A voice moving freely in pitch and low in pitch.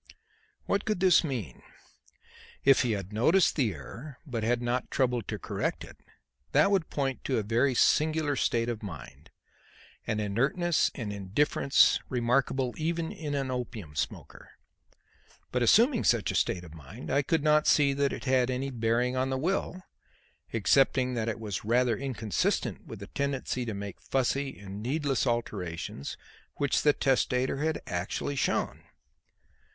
No: average, 4.2 semitones; low, 125 Hz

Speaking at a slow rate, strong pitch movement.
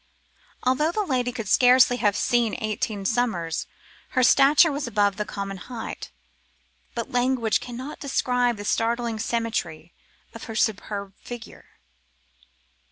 No: slow, 125 wpm; average, 3.1 semitones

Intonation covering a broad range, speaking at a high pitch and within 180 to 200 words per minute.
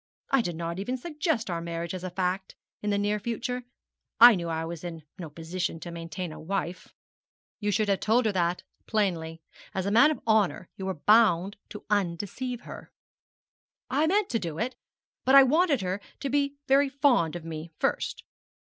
Yes: wide, 6.4 semitones; high, 200 Hz; average, 190 wpm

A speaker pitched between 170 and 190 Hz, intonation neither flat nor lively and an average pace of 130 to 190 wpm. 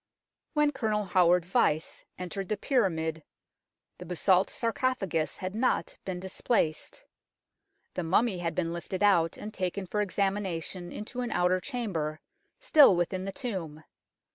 Yes: medium, 185 Hz; average, 3.6 semitones; average, 140 wpm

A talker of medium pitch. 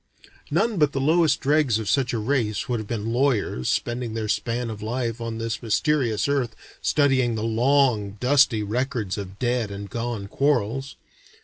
No: low, 120 Hz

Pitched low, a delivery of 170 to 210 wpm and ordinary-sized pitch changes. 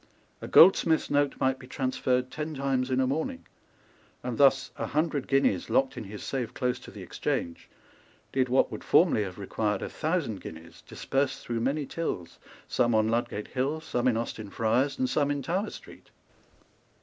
Yes: low, 130 Hz; average, 175 wpm; average, 4.1 semitones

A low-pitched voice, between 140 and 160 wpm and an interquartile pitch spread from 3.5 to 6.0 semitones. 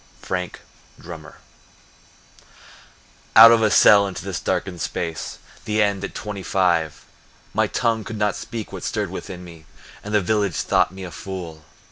No: very low, 95 Hz; average, 155 wpm; average, 3.1 semitones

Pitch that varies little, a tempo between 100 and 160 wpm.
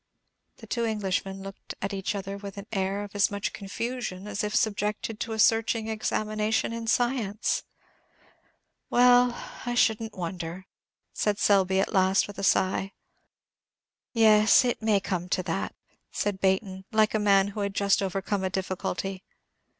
Yes: narrow, 2.2 semitones; average, 155 wpm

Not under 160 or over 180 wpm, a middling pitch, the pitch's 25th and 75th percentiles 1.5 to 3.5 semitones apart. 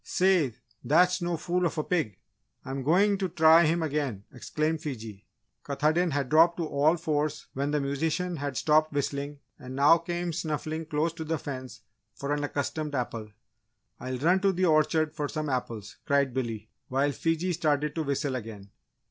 Yes: average, 175 wpm; medium, 150 Hz; average, 3.1 semitones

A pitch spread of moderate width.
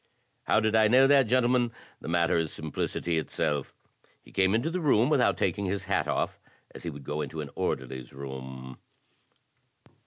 No: wide, 8.3 semitones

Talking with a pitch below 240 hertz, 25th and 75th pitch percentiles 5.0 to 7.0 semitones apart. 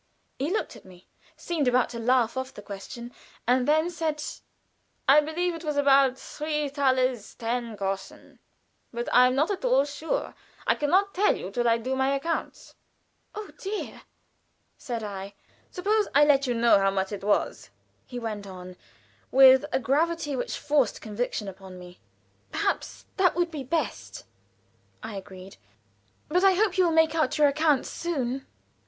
No: very high, 265 Hz; wide, 5.4 semitones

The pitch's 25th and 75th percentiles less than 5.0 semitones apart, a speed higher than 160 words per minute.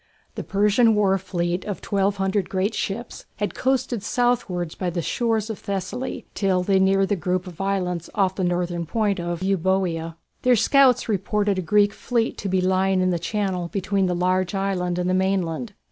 Yes: narrow, 2.4 semitones; average, 180 wpm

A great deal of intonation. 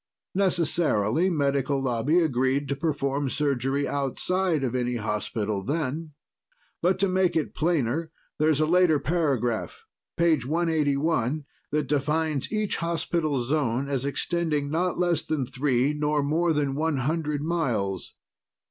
No: average, 3.5 semitones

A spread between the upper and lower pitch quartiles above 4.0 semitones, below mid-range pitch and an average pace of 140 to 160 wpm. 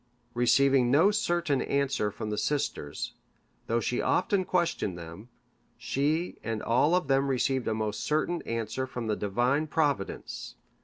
Yes: average, 5.1 semitones; low, 130 Hz; average, 145 wpm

